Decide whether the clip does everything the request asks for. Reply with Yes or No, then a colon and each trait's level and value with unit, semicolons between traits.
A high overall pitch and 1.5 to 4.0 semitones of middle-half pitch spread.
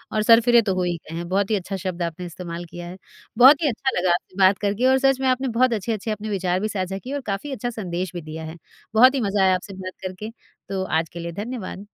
No: high, 195 Hz; average, 4.5 semitones